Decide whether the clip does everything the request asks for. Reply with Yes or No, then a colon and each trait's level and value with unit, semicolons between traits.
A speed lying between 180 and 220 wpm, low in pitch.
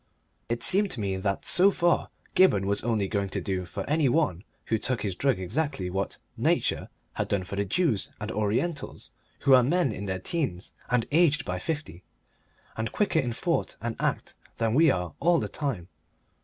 Yes: average, 190 wpm; low, 115 Hz